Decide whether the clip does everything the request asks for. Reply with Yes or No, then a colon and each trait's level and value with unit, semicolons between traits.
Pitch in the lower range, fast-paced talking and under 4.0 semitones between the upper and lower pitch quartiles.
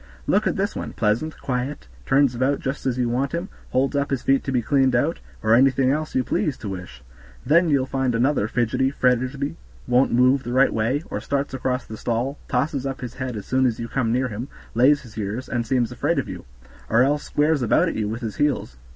Yes: low, 130 Hz; fast, 230 wpm; average, 2.7 semitones